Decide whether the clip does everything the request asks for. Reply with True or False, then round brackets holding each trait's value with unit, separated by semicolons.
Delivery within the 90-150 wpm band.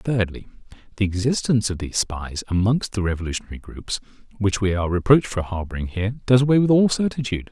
False (175 wpm)